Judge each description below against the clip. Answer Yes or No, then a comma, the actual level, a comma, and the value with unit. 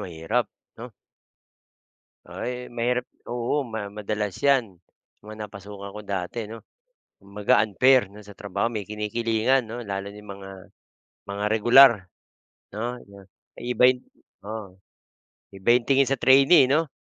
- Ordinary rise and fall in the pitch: Yes, average, 3.5 semitones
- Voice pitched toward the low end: Yes, low, 110 Hz